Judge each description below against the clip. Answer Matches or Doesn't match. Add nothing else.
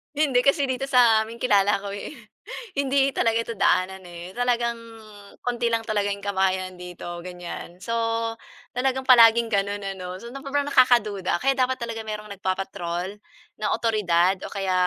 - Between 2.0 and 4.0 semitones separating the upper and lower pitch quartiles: Doesn't match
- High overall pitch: Matches